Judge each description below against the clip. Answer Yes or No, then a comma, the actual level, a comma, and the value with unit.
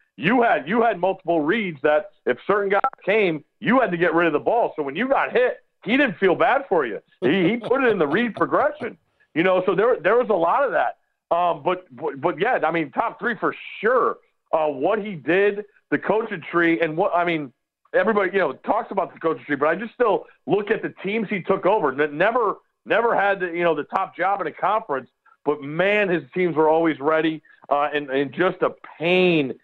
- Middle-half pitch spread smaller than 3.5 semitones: No, average, 4.7 semitones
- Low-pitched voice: No, medium, 175 Hz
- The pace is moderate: No, fast, 230 wpm